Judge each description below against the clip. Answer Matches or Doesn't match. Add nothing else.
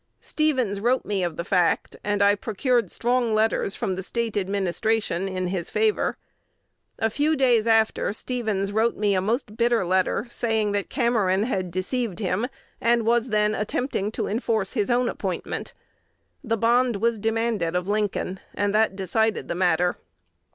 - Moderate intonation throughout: Matches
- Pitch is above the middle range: Matches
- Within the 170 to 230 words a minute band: Doesn't match